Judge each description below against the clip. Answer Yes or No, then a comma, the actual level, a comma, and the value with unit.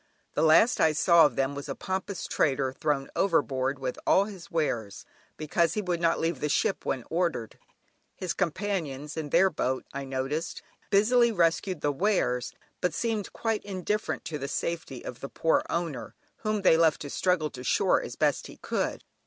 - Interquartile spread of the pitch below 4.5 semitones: No, average, 5.3 semitones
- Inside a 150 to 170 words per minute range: No, average, 180 wpm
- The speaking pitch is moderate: Yes, medium, 165 Hz